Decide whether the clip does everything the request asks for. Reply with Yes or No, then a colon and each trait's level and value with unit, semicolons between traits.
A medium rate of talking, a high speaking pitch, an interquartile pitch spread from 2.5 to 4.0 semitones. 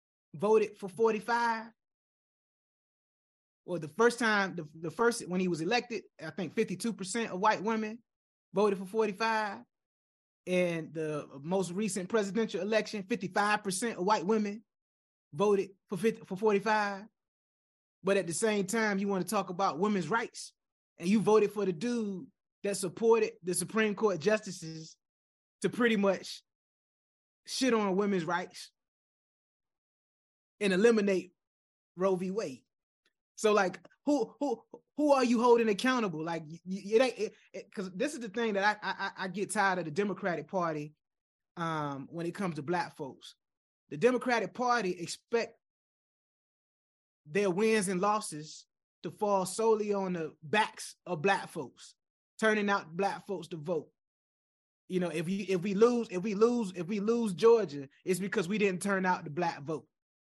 Yes: average, 155 wpm; high, 200 Hz; average, 3.6 semitones